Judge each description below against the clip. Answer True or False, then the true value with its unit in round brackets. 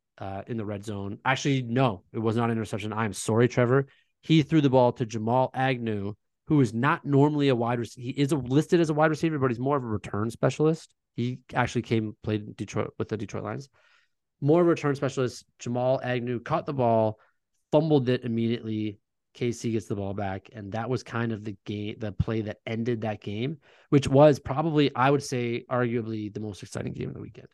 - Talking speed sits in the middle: False (215 wpm)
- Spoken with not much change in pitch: False (3.8 semitones)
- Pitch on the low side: True (120 Hz)